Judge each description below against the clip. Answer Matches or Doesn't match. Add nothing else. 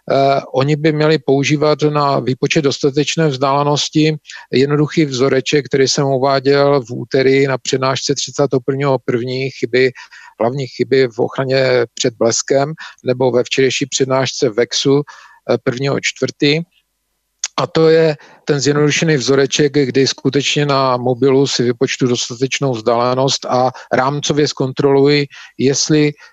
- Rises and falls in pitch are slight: Matches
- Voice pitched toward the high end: Doesn't match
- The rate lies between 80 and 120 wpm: Matches